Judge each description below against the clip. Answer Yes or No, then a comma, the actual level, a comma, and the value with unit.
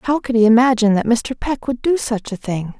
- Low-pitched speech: No, high, 235 Hz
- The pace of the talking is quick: Yes, fast, 260 wpm